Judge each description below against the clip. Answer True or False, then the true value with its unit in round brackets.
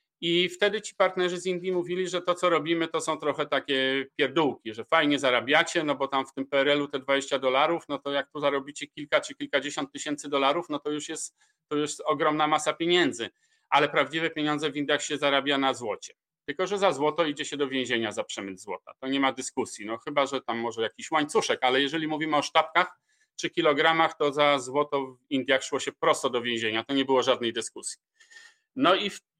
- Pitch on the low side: False (150 Hz)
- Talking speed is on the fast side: True (210 wpm)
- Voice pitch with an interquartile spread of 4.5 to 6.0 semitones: False (3.7 semitones)